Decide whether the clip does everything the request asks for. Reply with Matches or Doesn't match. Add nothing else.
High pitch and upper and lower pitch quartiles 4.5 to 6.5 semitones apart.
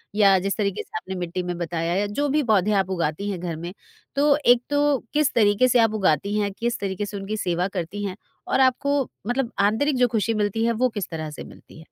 Matches